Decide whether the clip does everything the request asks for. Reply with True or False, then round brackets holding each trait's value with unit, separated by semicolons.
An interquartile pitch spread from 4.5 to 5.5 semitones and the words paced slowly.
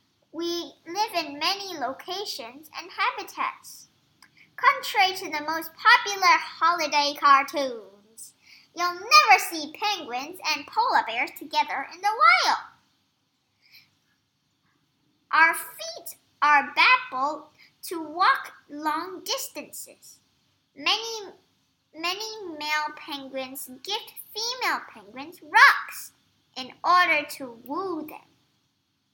True (5.1 semitones; 95 wpm)